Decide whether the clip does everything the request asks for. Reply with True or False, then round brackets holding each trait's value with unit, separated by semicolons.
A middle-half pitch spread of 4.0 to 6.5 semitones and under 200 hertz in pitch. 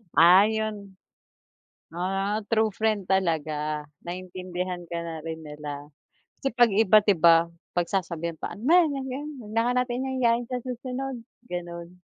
True (4.8 semitones; 190 Hz)